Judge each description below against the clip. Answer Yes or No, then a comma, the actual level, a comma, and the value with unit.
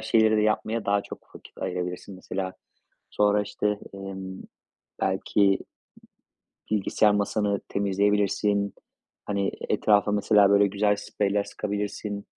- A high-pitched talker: No, low, 100 Hz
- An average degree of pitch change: No, narrow, 0.9 semitones